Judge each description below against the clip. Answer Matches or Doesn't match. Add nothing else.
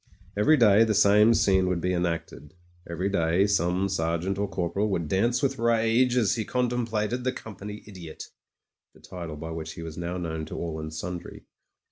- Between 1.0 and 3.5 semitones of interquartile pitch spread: Doesn't match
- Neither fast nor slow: Doesn't match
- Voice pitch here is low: Matches